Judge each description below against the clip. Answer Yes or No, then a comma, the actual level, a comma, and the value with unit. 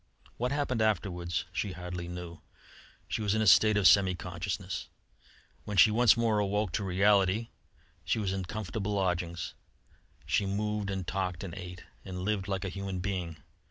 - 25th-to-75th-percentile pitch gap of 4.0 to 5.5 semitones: No, average, 2.7 semitones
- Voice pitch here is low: Yes, very low, 95 Hz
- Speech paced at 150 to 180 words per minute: Yes, average, 165 wpm